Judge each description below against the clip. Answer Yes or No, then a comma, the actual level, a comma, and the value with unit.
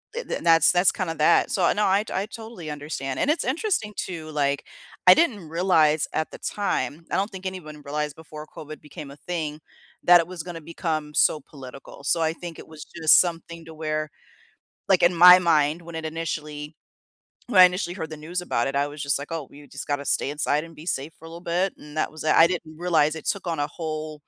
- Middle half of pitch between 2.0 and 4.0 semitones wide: Yes, average, 2.9 semitones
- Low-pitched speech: No, medium, 160 Hz